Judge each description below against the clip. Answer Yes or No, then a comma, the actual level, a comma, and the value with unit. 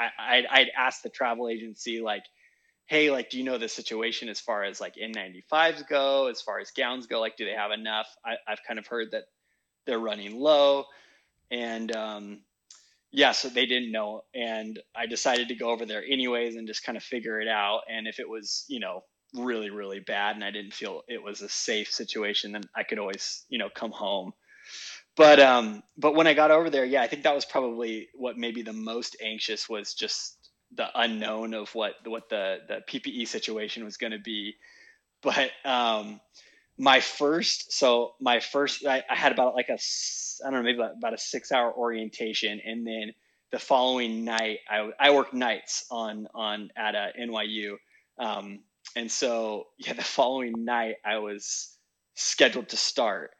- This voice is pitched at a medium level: No, low, 115 Hz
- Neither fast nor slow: Yes, average, 190 wpm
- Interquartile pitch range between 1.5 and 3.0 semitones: Yes, narrow, 2.5 semitones